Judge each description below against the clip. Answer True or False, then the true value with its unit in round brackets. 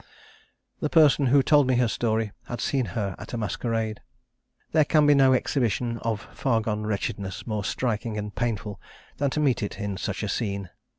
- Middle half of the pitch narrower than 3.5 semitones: False (3.9 semitones)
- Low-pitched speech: True (115 Hz)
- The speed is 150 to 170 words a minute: False (185 wpm)